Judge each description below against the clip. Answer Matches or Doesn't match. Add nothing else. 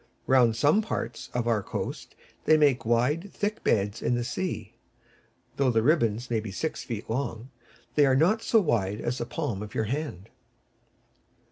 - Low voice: Matches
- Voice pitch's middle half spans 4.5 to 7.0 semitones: Matches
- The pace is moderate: Matches